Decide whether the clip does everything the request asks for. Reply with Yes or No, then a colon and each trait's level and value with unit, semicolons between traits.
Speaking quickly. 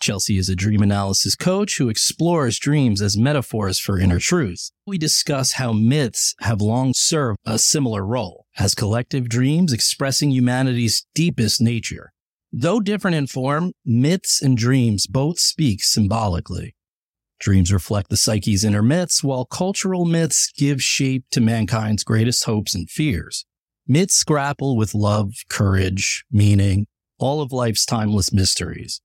No: average, 145 wpm